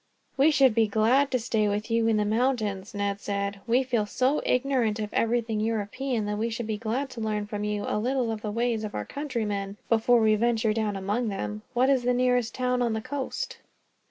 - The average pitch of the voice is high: Yes, high, 225 Hz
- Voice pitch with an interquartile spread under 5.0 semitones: Yes, average, 3.0 semitones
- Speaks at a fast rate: Yes, fast, 220 wpm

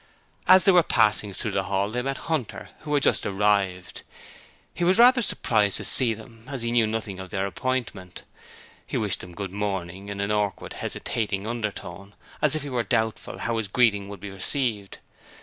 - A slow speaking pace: No, average, 190 wpm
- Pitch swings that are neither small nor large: Yes, average, 4.1 semitones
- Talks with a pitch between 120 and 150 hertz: No, low, 110 Hz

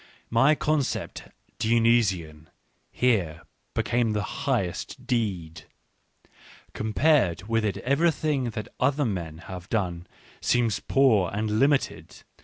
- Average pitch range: No, wide, 5.9 semitones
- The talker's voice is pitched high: No, low, 110 Hz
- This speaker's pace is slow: Yes, slow, 110 wpm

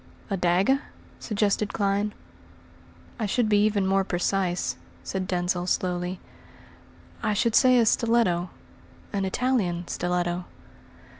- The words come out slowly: Yes, slow, 115 wpm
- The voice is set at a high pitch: Yes, high, 195 Hz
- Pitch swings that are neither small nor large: Yes, average, 3.2 semitones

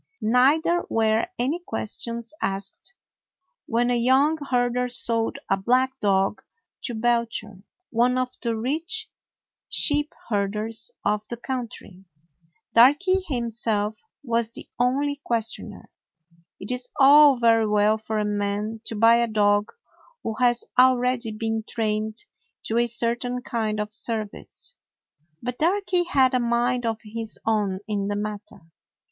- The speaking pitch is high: Yes, high, 235 Hz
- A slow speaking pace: Yes, slow, 130 wpm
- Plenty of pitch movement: No, average, 2.8 semitones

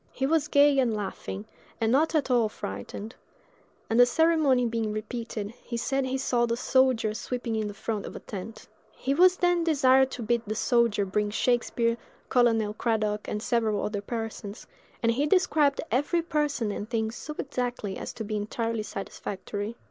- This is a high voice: Yes, high, 235 Hz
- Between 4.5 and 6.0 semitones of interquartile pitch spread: No, average, 3.8 semitones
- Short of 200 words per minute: Yes, average, 175 wpm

